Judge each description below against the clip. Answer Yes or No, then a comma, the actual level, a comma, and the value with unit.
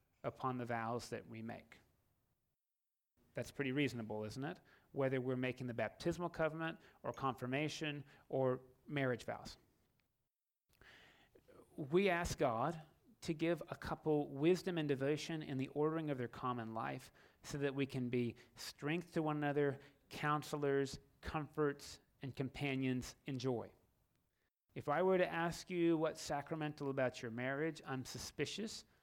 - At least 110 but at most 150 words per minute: Yes, average, 140 wpm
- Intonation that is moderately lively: Yes, average, 3.6 semitones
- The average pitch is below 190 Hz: Yes, medium, 140 Hz